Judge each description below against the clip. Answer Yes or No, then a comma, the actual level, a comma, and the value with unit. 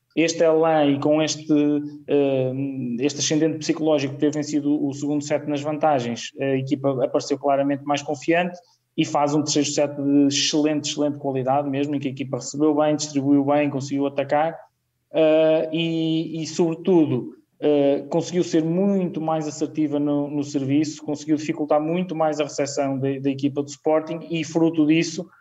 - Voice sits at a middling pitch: Yes, medium, 150 Hz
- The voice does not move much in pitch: Yes, narrow, 1.9 semitones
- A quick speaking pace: No, average, 155 wpm